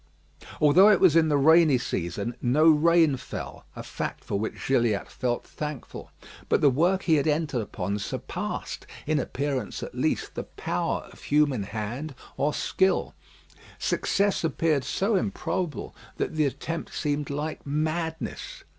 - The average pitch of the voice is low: No, medium, 150 Hz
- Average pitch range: Yes, average, 4.1 semitones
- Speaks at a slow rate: No, average, 145 wpm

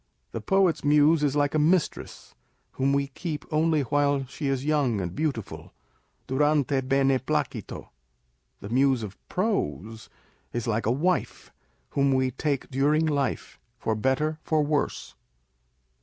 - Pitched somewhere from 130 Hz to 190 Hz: Yes, medium, 140 Hz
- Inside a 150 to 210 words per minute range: No, average, 140 wpm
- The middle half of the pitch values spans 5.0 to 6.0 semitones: No, average, 3.1 semitones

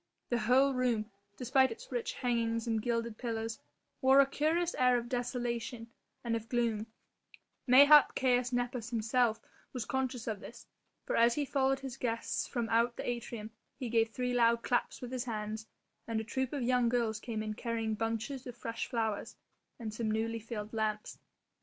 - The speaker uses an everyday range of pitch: No, narrow, 1.9 semitones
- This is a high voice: Yes, high, 235 Hz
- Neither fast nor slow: Yes, average, 175 wpm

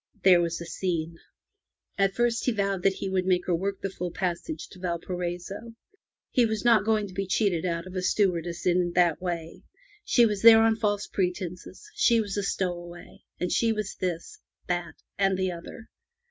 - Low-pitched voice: No, medium, 185 Hz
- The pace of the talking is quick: No, average, 185 wpm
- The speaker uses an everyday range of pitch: Yes, average, 3.1 semitones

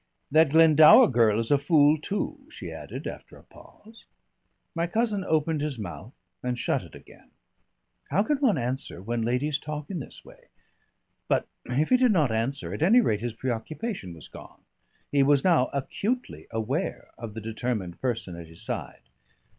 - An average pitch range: No, wide, 6.4 semitones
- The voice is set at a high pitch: No, medium, 140 Hz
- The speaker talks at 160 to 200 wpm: Yes, average, 170 wpm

